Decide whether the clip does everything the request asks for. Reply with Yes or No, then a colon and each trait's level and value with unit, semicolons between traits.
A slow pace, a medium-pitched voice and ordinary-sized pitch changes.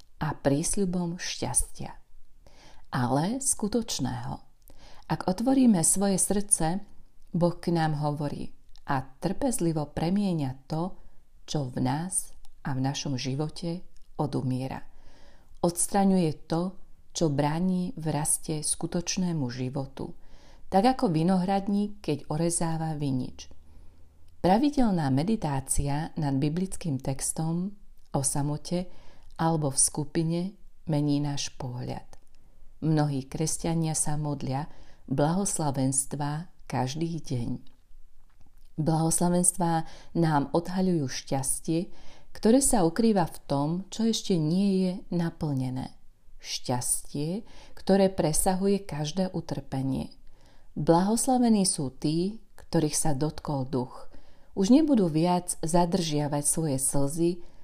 Yes: slow, 95 wpm; medium, 160 Hz; average, 4.5 semitones